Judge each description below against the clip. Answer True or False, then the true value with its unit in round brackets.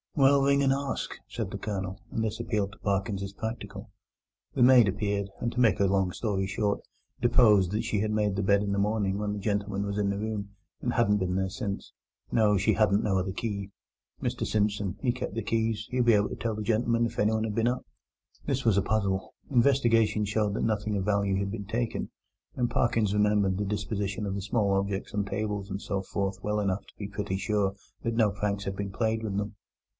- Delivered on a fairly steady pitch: True (2.1 semitones)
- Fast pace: True (220 wpm)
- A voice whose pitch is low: True (105 Hz)